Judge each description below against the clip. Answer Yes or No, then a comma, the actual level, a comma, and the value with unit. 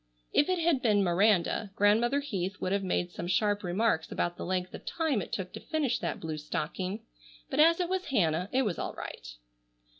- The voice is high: Yes, high, 200 Hz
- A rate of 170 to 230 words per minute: Yes, fast, 205 wpm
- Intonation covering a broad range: Yes, wide, 6.6 semitones